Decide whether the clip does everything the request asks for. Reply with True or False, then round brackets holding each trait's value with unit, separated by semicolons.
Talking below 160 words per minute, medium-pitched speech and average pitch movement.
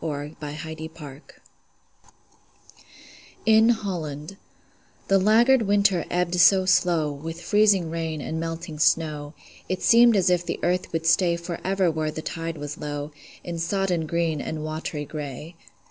True (145 wpm; 165 Hz; 3.2 semitones)